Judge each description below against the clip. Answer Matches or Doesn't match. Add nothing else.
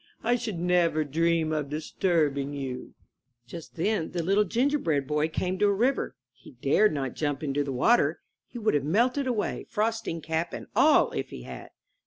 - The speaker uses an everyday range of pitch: Doesn't match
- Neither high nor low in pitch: Matches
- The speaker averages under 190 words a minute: Matches